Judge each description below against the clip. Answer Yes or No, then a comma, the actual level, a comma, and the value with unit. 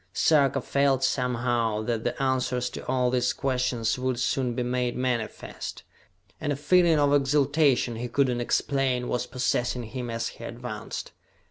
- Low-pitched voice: Yes, low, 125 Hz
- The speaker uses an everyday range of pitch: No, narrow, 2.0 semitones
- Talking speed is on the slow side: No, average, 155 wpm